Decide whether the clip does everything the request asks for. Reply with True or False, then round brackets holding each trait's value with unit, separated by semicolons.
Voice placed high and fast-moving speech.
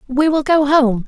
True (275 Hz; 225 wpm)